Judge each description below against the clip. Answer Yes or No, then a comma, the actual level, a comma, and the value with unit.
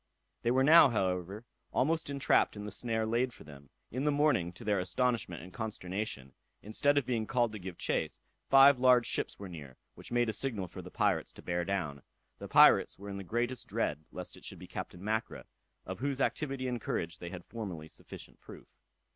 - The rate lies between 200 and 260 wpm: Yes, fast, 205 wpm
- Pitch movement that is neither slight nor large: No, wide, 5.9 semitones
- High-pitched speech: No, low, 110 Hz